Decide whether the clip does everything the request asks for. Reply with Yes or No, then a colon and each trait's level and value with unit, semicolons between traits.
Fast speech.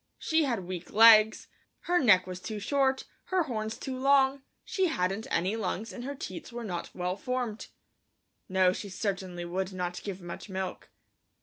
No: average, 170 wpm